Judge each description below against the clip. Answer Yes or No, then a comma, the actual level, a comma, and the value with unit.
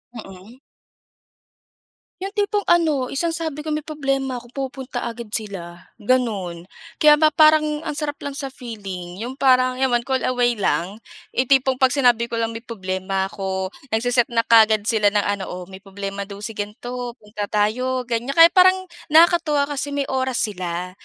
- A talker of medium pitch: No, high, 245 Hz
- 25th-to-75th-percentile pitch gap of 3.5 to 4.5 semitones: No, average, 5.2 semitones